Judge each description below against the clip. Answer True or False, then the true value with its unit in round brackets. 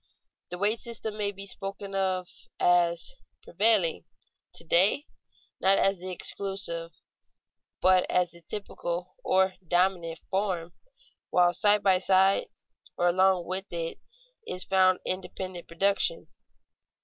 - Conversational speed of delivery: False (120 wpm)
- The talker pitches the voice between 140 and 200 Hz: True (185 Hz)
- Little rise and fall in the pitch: True (2.0 semitones)